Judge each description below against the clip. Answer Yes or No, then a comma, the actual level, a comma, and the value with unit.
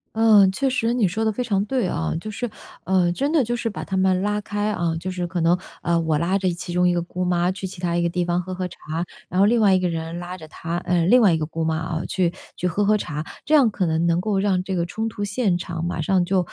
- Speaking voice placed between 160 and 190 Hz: Yes, medium, 185 Hz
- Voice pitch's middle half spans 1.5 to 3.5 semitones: Yes, average, 3.2 semitones